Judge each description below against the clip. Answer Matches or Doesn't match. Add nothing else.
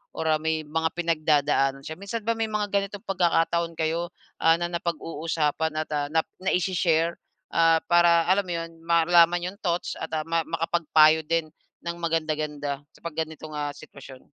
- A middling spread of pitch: Doesn't match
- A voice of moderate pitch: Matches